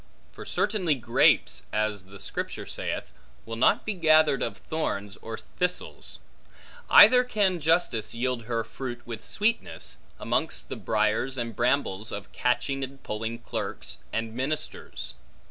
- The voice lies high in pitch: No, low, 120 Hz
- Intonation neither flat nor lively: No, wide, 5.9 semitones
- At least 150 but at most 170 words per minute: No, slow, 135 wpm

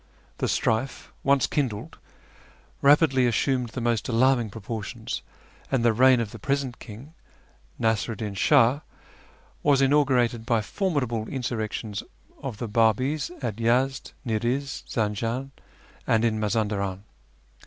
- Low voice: Yes, low, 120 Hz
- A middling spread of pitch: Yes, average, 3.3 semitones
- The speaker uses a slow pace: Yes, slow, 120 wpm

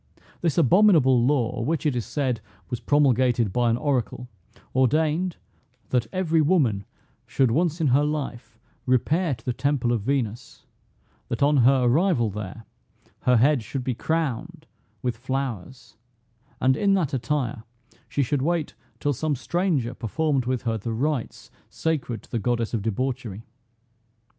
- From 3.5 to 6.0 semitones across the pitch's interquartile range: Yes, average, 4.2 semitones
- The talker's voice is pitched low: Yes, low, 130 Hz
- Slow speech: No, average, 150 wpm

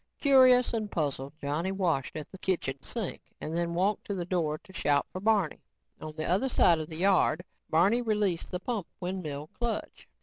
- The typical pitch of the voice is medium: Yes, medium, 180 Hz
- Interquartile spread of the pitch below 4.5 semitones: No, average, 4.9 semitones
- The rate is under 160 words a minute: No, average, 190 wpm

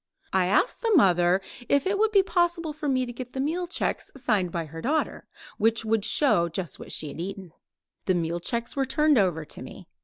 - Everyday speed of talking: No, fast, 215 wpm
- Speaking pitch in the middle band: No, high, 235 Hz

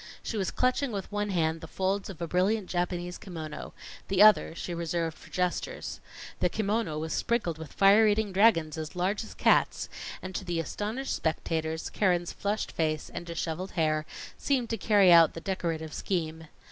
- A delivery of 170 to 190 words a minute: Yes, average, 175 wpm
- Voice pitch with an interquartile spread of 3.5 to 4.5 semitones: Yes, average, 4.0 semitones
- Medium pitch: Yes, medium, 180 Hz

